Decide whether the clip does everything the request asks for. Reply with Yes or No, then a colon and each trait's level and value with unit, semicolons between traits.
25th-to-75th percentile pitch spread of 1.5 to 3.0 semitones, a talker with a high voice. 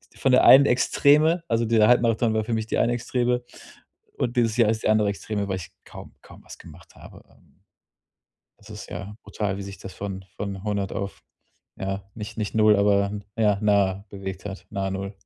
No: average, 2.7 semitones; low, 105 Hz